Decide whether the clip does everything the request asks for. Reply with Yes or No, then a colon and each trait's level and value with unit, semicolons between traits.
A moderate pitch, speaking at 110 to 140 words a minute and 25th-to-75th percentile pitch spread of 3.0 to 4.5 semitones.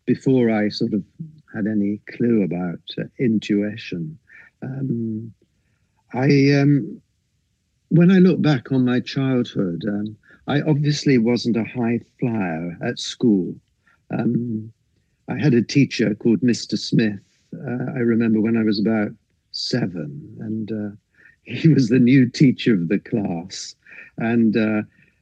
No: low, 115 Hz; slow, 135 wpm; average, 3.6 semitones